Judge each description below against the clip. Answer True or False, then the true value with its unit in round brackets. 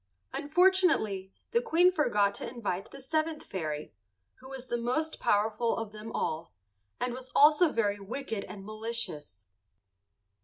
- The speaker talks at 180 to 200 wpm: False (140 wpm)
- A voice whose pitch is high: True (235 Hz)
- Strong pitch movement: True (6.8 semitones)